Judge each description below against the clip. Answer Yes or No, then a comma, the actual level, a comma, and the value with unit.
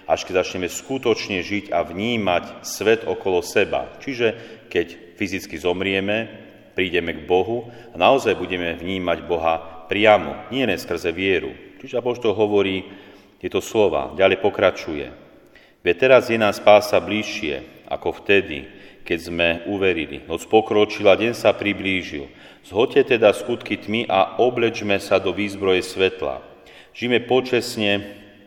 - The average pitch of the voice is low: Yes, low, 100 Hz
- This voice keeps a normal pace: Yes, average, 130 wpm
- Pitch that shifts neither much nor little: Yes, average, 3.1 semitones